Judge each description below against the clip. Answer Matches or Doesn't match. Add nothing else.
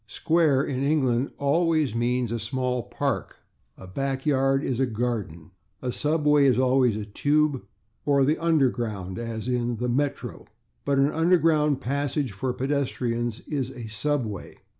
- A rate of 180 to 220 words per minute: Doesn't match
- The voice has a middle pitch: Doesn't match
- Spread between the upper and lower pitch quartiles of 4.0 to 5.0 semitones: Doesn't match